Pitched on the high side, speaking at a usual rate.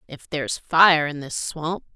No: medium, 155 Hz; average, 185 wpm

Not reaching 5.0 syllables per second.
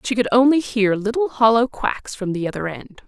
No: 5.4 syllables/s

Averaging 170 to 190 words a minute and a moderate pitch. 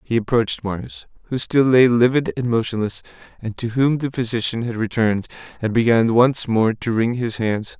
No: average, 185 wpm; low, 115 Hz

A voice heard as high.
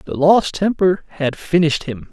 No: medium, 165 Hz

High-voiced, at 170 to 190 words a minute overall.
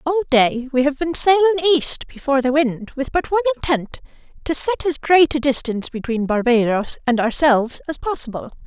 Yes: very high, 285 Hz; average, 175 wpm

